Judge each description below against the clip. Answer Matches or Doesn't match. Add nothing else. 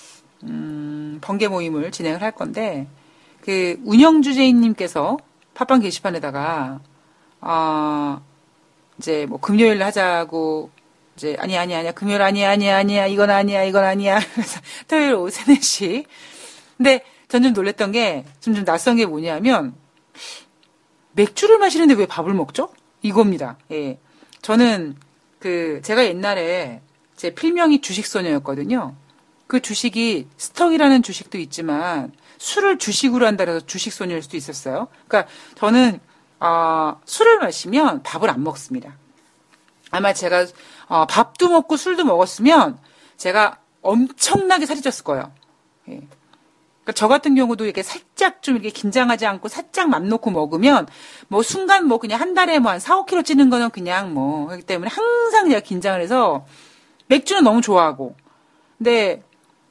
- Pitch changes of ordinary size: Doesn't match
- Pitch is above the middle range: Matches